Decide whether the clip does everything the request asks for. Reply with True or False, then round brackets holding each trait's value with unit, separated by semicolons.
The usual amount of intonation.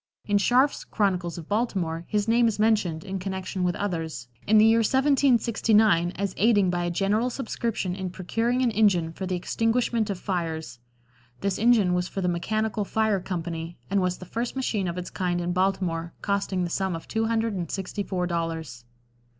True (3.9 semitones)